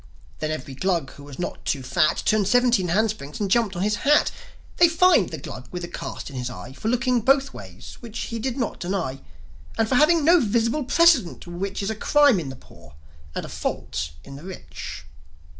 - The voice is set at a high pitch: Yes, high, 200 Hz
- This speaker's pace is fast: Yes, fast, 210 wpm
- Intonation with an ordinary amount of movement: No, wide, 8.9 semitones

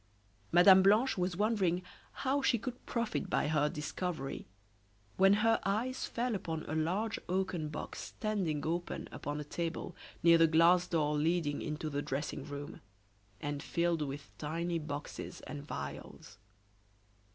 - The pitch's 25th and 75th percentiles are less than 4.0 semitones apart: No, average, 4.5 semitones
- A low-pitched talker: No, medium, 170 Hz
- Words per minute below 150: Yes, average, 140 wpm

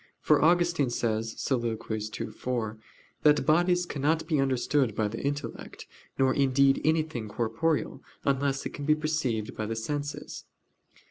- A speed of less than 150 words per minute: Yes, average, 140 wpm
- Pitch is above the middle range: No, medium, 140 Hz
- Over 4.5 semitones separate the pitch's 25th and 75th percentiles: Yes, average, 4.9 semitones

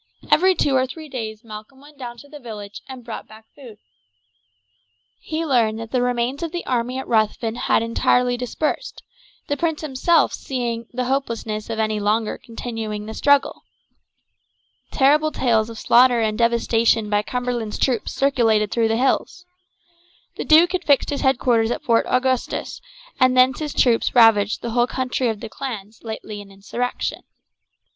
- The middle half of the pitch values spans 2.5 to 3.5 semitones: Yes, average, 3.2 semitones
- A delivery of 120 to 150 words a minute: No, average, 165 wpm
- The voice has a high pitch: Yes, high, 240 Hz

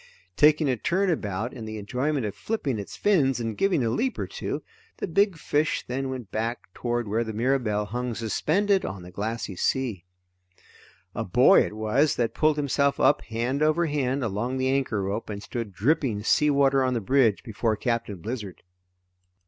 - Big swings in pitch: No, average, 4.6 semitones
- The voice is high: No, low, 125 Hz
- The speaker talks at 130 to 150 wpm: No, average, 180 wpm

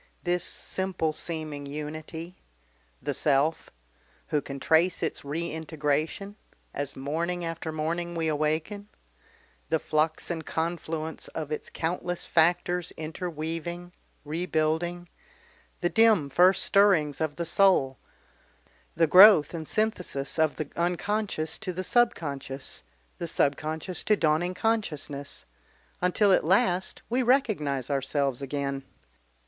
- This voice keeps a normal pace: No, slow, 115 wpm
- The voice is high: No, medium, 160 Hz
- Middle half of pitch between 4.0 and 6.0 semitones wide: No, average, 2.9 semitones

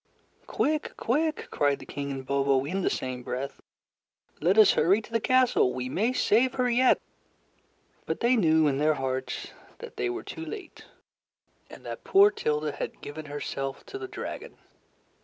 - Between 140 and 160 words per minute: No, average, 170 wpm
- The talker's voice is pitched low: No, medium, 170 Hz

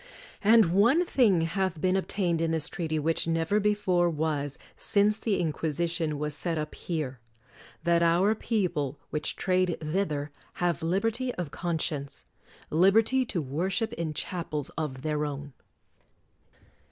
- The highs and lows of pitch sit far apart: No, average, 4.1 semitones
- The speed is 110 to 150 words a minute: Yes, average, 145 wpm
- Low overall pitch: No, medium, 170 Hz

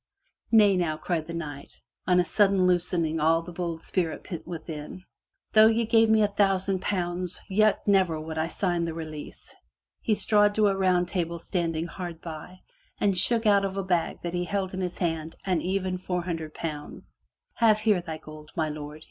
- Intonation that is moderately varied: Yes, average, 3.2 semitones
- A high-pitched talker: No, medium, 180 Hz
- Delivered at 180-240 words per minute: Yes, average, 190 wpm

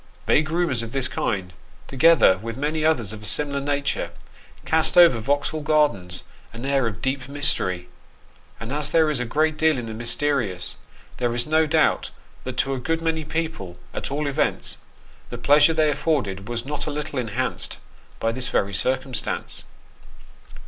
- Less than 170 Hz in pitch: Yes, medium, 140 Hz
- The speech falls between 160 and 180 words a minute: Yes, average, 170 wpm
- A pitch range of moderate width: Yes, average, 4.7 semitones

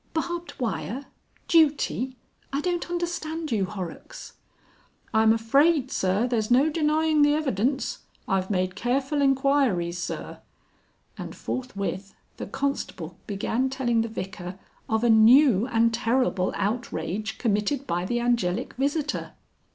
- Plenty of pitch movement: Yes, wide, 5.9 semitones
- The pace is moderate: No, slow, 120 wpm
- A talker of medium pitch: No, high, 240 Hz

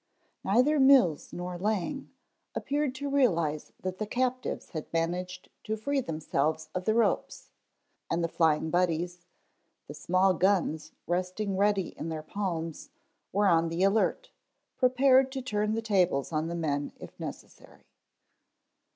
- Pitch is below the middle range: No, medium, 185 Hz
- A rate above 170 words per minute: No, average, 140 wpm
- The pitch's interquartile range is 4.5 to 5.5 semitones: Yes, average, 5.2 semitones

